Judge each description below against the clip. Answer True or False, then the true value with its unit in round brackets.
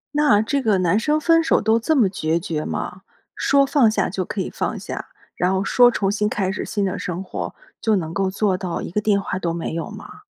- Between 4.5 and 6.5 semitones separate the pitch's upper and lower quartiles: False (4.0 semitones)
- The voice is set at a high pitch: True (200 Hz)